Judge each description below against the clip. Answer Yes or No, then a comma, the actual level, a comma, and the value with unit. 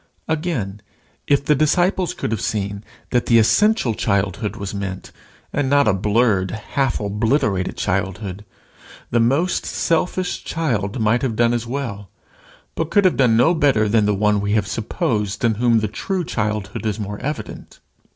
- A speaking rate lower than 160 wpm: No, average, 165 wpm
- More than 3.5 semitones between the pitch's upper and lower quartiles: Yes, average, 5.3 semitones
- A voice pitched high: No, low, 110 Hz